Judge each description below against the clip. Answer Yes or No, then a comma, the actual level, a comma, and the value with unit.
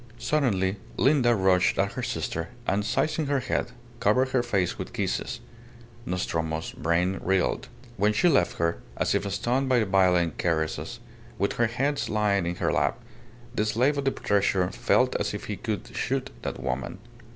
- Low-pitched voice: Yes, low, 100 Hz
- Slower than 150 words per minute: No, average, 170 wpm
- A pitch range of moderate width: No, wide, 5.9 semitones